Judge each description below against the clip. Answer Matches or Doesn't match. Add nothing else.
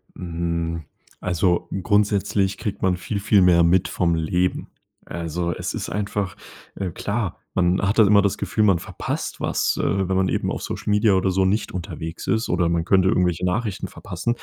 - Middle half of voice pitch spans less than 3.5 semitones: Matches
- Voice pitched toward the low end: Matches